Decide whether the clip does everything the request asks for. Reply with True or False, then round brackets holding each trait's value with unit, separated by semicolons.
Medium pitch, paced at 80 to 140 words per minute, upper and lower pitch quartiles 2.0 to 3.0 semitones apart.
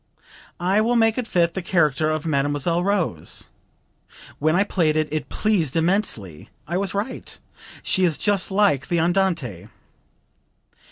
False (170 Hz; 135 wpm; 4.4 semitones)